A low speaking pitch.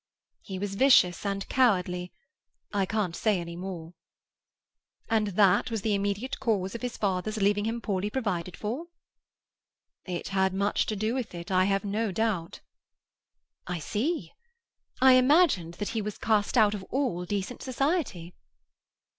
No: high, 205 Hz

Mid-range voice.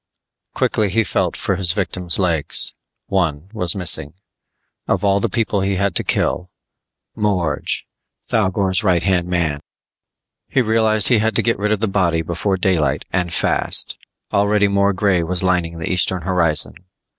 No: very low, 95 Hz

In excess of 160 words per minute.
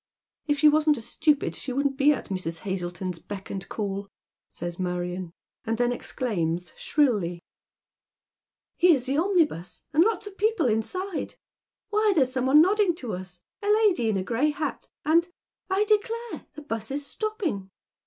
Yes: average, 175 wpm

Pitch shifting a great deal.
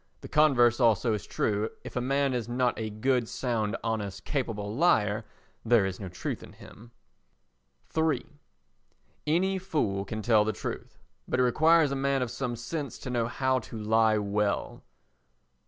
No: average, 4.0 semitones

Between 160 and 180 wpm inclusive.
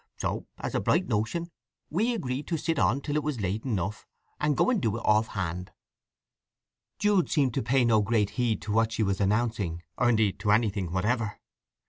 No: average, 195 wpm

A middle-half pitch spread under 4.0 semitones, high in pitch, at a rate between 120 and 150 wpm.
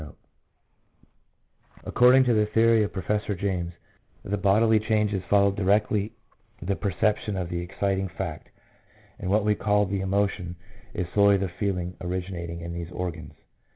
No: narrow, 2.5 semitones; low, 100 Hz; average, 145 wpm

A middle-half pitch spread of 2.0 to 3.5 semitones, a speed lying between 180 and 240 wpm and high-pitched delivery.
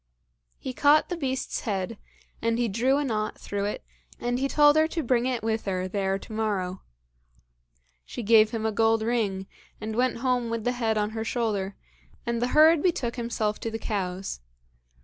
Yes: average, 3.0 semitones; average, 190 wpm; high, 225 Hz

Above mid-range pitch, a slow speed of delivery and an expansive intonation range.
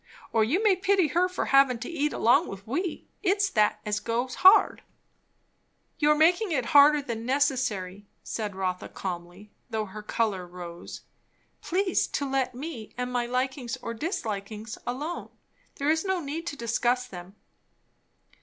No: very high, 250 Hz; average, 155 wpm; wide, 6.6 semitones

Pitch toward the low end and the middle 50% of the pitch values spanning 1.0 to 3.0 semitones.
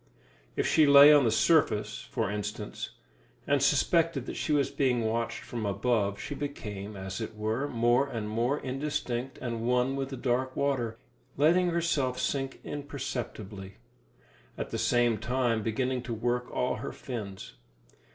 No: low, 125 Hz; average, 3.8 semitones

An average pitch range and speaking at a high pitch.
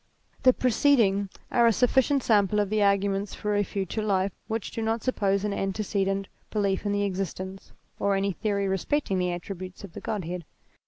No: narrow, 2.0 semitones; high, 200 Hz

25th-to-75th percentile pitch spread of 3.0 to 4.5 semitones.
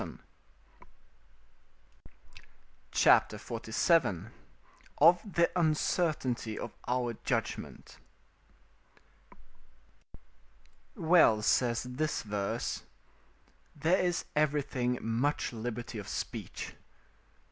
No: wide, 5.6 semitones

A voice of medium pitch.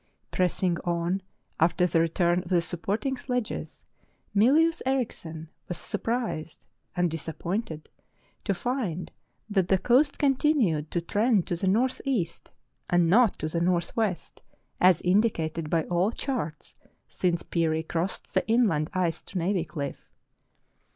Yes: medium, 180 Hz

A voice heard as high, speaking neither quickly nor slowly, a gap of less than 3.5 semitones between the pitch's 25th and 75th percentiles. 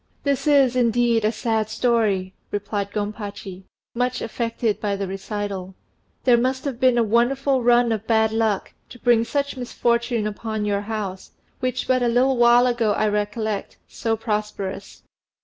Yes: high, 225 Hz; average, 155 wpm; average, 2.7 semitones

